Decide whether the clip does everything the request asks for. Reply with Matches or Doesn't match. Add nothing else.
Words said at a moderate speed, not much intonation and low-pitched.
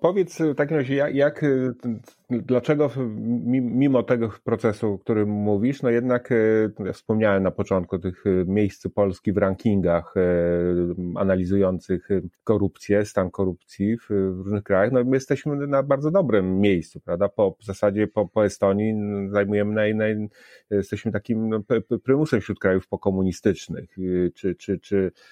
Doesn't match